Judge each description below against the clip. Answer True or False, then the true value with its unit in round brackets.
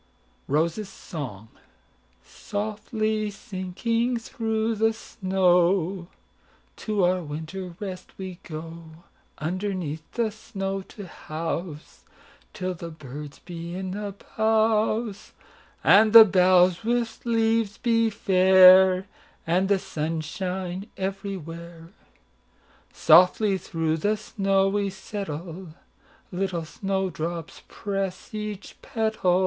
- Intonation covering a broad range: False (3.7 semitones)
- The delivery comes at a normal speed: False (85 wpm)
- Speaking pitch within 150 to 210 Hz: True (190 Hz)